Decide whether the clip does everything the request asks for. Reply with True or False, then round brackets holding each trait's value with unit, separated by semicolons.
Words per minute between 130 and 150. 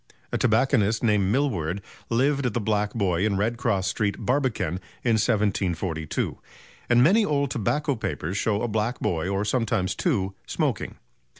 True (145 wpm)